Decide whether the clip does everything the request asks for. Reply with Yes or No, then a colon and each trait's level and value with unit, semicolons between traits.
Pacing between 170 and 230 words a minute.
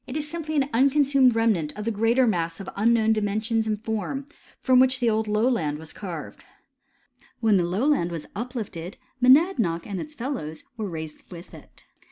Yes: average, 175 wpm